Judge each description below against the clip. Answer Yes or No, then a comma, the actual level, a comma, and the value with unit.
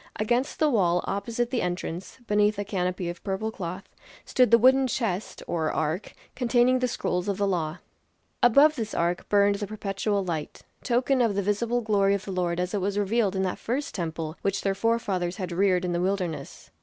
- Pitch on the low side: No, high, 200 Hz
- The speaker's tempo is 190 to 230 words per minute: Yes, average, 195 wpm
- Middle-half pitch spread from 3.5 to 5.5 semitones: Yes, average, 4.2 semitones